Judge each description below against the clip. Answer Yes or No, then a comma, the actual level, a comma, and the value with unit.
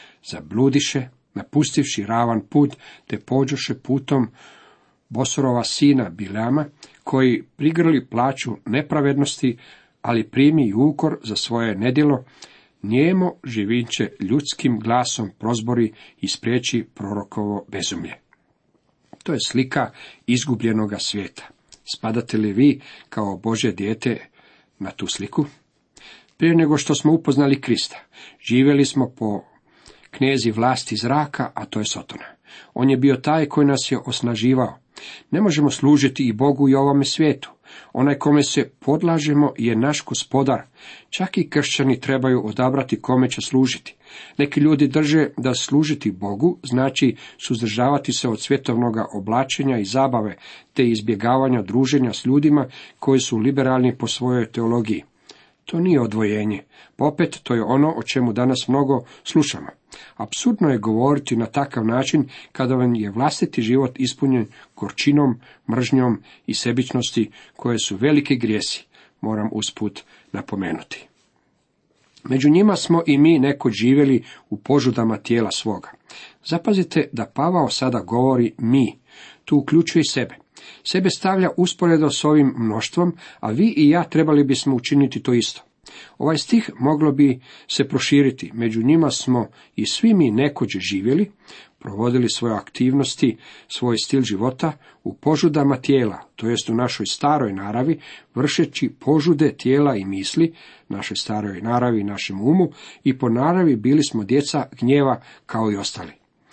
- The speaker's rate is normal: Yes, average, 135 wpm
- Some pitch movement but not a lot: Yes, average, 3.8 semitones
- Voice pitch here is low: Yes, low, 130 Hz